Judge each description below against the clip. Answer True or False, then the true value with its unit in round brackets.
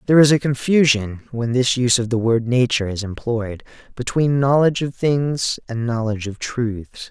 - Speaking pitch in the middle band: False (125 Hz)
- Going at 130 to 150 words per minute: False (175 wpm)